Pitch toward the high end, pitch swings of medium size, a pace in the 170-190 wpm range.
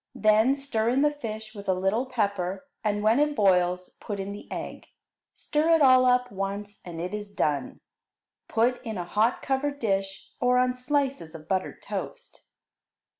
Yes: high, 215 Hz; average, 4.6 semitones; average, 175 wpm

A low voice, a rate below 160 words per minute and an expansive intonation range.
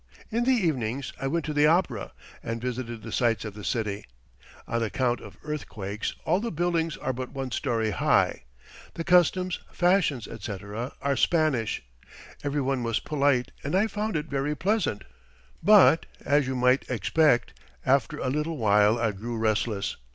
No: low, 130 Hz; average, 165 wpm; wide, 5.7 semitones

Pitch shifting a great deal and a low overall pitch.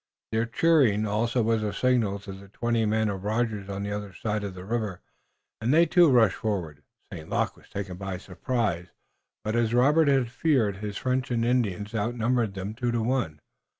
No: average, 3.3 semitones; low, 110 Hz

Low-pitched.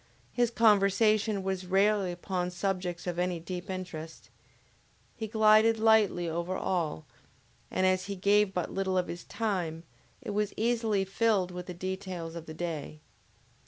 No: high, 190 Hz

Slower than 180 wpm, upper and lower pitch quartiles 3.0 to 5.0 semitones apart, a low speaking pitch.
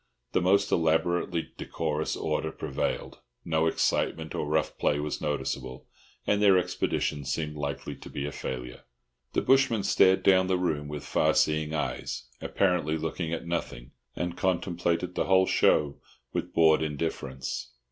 Yes: average, 145 wpm; average, 3.4 semitones; very low, 80 Hz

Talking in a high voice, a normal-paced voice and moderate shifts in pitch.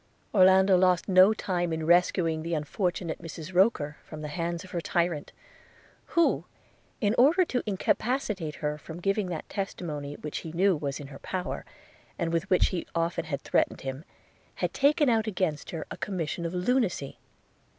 No: medium, 175 Hz; average, 170 wpm; average, 3.5 semitones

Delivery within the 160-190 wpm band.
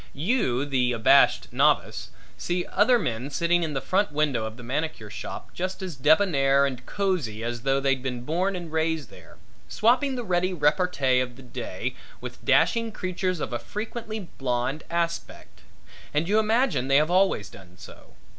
Yes: average, 170 wpm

